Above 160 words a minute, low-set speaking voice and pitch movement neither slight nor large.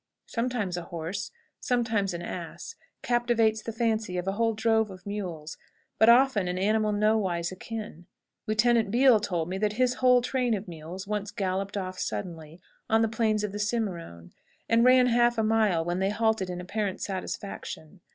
No: average, 170 wpm; high, 210 Hz; average, 3.6 semitones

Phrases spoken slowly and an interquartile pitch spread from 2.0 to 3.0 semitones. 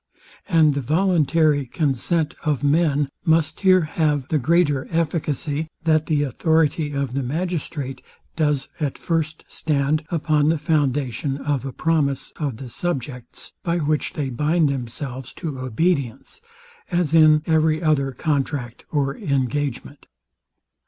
Yes: slow, 130 wpm; average, 2.7 semitones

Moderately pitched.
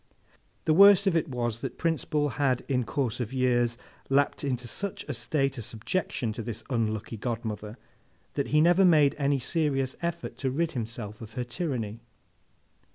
No: low, 130 Hz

